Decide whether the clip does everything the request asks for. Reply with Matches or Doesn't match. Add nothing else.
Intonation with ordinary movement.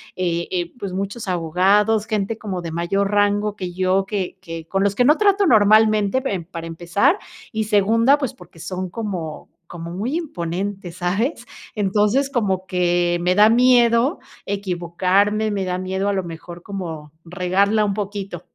Matches